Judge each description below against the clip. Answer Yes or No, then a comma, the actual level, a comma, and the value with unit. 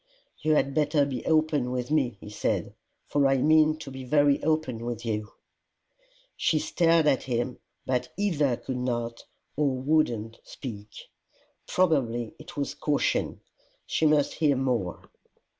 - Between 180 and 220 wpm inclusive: No, average, 145 wpm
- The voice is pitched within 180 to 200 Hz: No, low, 135 Hz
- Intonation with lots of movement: No, average, 4.1 semitones